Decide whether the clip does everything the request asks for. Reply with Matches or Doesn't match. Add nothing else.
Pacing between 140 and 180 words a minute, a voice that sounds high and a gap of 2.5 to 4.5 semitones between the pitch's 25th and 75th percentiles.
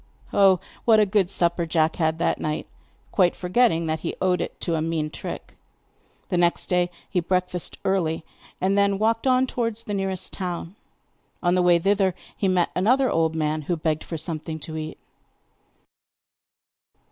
Doesn't match